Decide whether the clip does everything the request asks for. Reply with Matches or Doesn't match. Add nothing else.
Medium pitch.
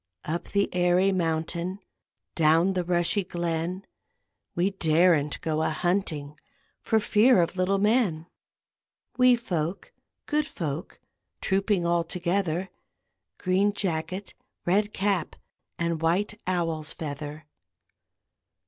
Matches